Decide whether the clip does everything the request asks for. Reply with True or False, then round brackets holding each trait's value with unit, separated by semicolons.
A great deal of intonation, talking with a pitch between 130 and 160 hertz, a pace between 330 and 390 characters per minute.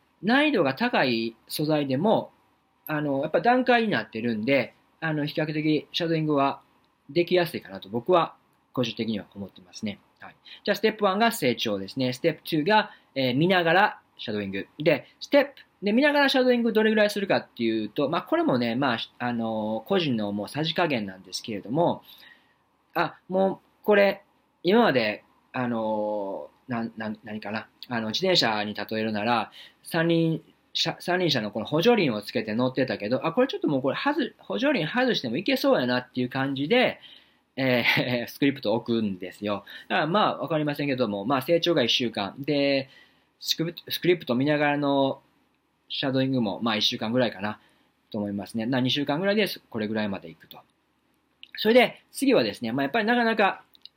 True (8.9 semitones; 140 Hz; 370 characters per minute)